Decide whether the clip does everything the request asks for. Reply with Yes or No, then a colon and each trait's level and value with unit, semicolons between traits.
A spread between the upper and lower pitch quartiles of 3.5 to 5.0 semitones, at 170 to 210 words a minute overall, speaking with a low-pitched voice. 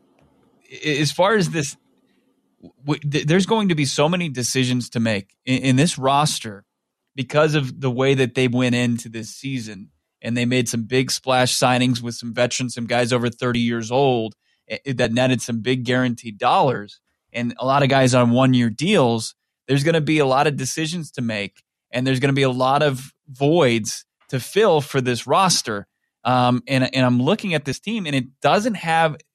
No: average, 3.0 semitones; average, 190 wpm; low, 130 Hz